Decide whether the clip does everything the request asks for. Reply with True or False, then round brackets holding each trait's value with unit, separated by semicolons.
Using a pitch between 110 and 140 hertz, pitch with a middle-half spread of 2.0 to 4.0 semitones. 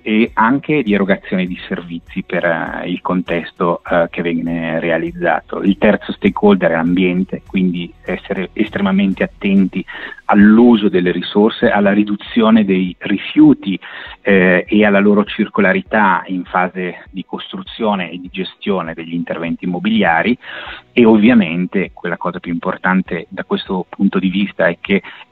False (95 Hz; 2.8 semitones)